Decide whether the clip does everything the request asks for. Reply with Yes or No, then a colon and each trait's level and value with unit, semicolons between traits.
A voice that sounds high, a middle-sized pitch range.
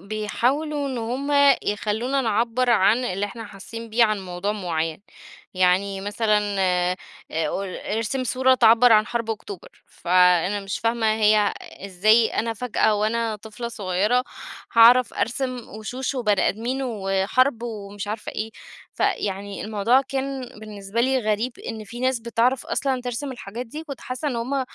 Yes: high, 225 Hz; average, 3.5 semitones